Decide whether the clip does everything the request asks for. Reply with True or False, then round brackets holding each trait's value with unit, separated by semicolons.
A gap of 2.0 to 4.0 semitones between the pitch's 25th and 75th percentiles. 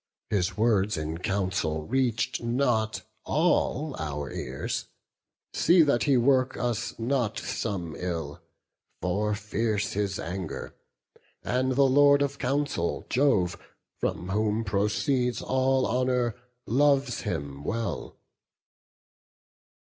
False (5.3 semitones)